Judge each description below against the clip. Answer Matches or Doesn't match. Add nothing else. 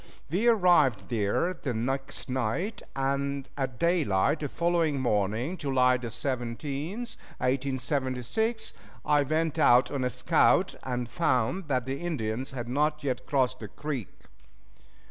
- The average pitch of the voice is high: Doesn't match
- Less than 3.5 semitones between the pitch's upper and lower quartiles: Doesn't match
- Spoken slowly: Matches